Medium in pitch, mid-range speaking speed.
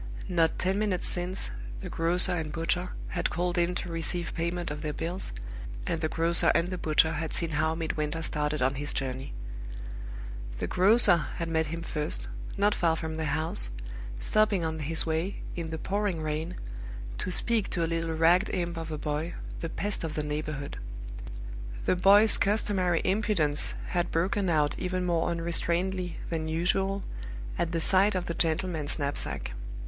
Yes: medium, 165 Hz; average, 170 wpm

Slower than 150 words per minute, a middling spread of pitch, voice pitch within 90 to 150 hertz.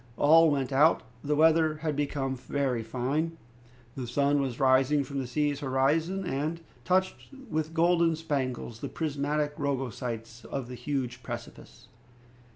Yes: average, 140 wpm; average, 3.2 semitones; medium, 140 Hz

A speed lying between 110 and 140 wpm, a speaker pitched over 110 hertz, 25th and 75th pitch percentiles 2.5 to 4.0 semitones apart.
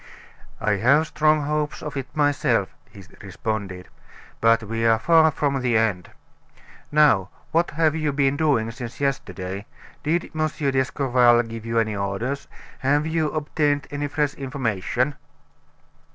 No: slow, 135 wpm; low, 135 Hz; average, 4.7 semitones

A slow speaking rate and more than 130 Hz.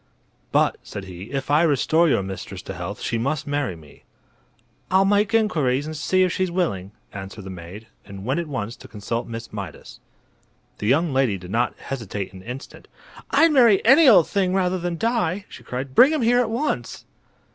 No: average, 190 wpm; medium, 140 Hz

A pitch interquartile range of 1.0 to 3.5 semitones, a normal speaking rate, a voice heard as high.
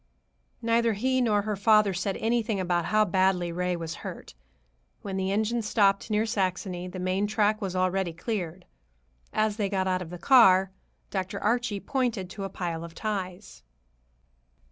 Yes: average, 2.8 semitones; average, 165 wpm; high, 195 Hz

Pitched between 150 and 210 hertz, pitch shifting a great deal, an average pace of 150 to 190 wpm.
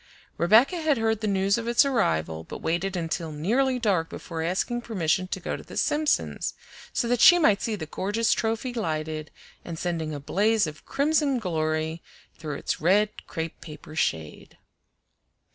Yes: high, 190 Hz; wide, 6.6 semitones; average, 165 wpm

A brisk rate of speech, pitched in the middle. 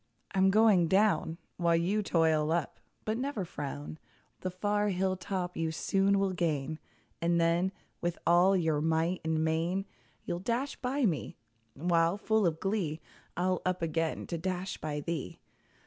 No: average, 155 wpm; medium, 175 Hz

